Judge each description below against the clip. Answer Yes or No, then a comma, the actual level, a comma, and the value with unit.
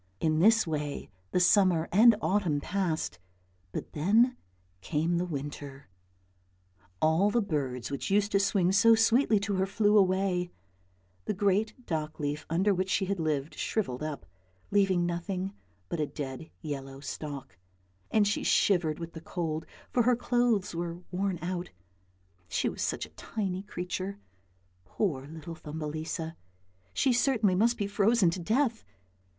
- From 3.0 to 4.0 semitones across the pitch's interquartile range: No, average, 4.6 semitones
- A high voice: No, medium, 180 Hz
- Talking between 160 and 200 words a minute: No, average, 145 wpm